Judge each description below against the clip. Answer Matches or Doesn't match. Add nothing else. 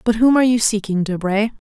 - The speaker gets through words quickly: Matches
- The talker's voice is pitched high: Matches